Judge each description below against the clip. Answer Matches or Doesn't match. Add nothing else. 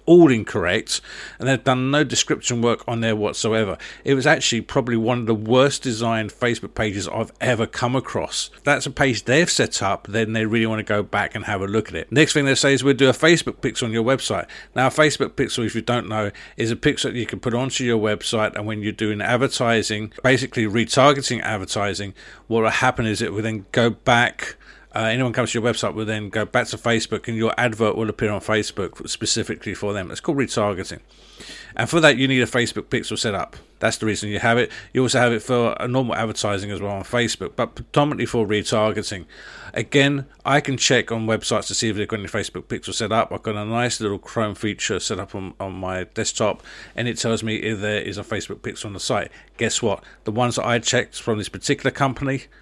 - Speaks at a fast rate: Matches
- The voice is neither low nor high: Doesn't match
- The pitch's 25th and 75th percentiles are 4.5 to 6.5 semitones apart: Doesn't match